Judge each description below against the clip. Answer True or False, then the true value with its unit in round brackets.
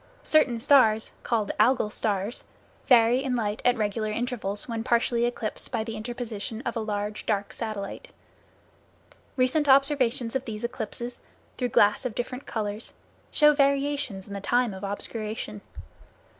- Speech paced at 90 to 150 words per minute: True (145 wpm)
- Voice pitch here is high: True (230 Hz)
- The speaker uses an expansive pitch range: False (3.0 semitones)